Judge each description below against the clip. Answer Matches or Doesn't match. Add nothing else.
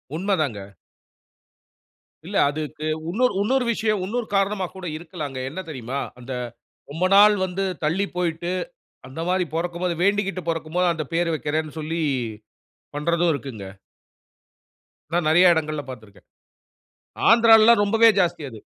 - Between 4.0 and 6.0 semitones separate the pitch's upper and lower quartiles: Matches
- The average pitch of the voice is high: Doesn't match